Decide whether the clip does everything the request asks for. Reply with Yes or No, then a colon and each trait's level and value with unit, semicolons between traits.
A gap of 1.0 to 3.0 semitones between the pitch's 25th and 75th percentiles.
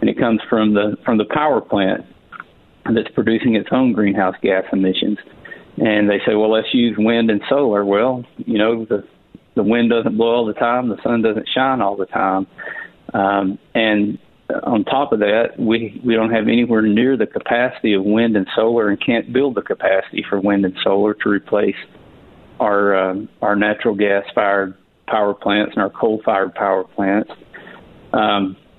Yes: narrow, 2.4 semitones